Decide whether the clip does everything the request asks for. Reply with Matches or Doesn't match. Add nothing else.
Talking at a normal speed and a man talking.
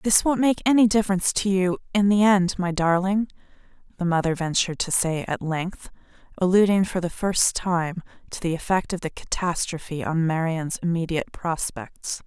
Doesn't match